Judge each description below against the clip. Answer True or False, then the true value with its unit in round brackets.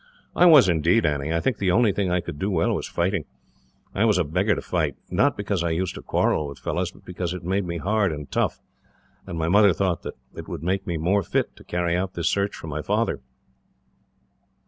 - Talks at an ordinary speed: False (230 wpm)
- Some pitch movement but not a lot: True (3.3 semitones)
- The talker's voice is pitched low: True (90 Hz)